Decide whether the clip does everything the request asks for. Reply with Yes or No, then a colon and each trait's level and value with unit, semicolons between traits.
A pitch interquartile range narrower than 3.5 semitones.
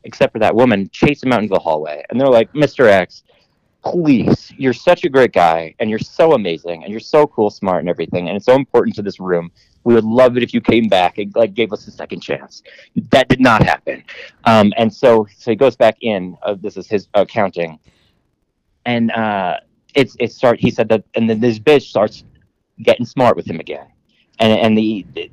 No: average, 3.8 semitones